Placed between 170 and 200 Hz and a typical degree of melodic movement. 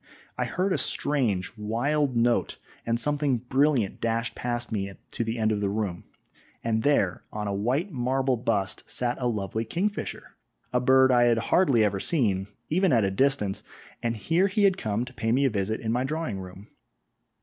No: low, 120 Hz; average, 4.4 semitones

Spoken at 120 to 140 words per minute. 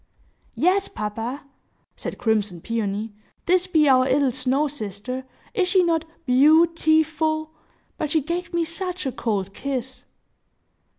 Yes: slow, 135 wpm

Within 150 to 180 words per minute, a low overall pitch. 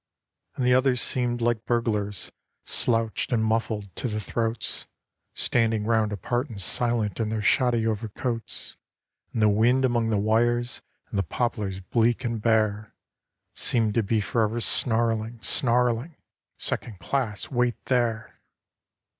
No: average, 140 wpm; low, 115 Hz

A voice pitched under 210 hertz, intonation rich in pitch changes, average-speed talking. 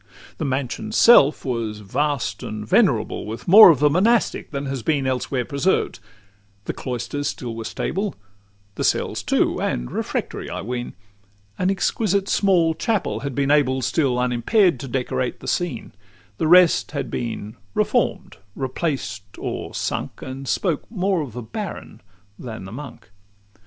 Yes: medium, 140 Hz; wide, 6.2 semitones; average, 150 wpm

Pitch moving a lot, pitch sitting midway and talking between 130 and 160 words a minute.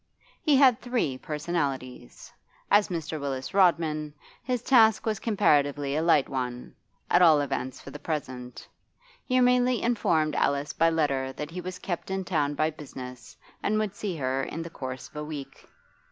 No: wide, 5.7 semitones; medium, 155 Hz; average, 170 wpm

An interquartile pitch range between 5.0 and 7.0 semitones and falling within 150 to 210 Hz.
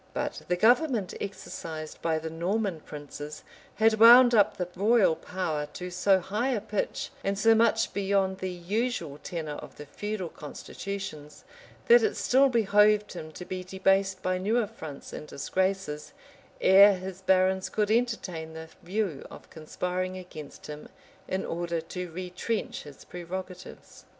No: average, 3.9 semitones; medium, 185 Hz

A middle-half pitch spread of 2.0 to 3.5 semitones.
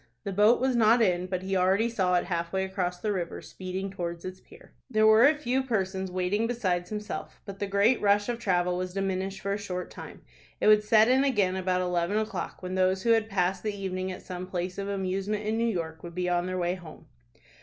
Yes: average, 2.7 semitones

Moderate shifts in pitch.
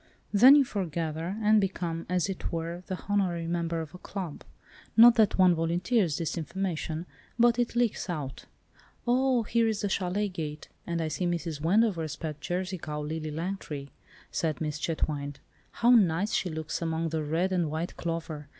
Yes: average, 3.7 semitones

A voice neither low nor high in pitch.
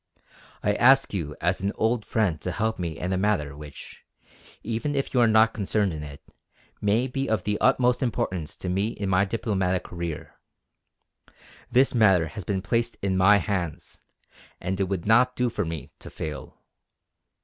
No: low, 100 Hz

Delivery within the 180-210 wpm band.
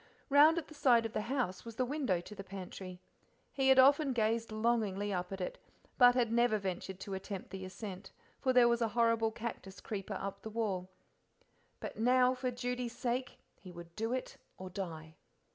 Yes: average, 195 wpm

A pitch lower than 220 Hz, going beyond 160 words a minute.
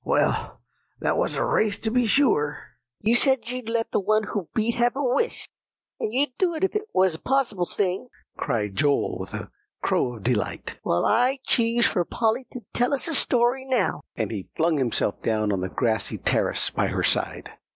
No: high, 225 Hz; average, 200 wpm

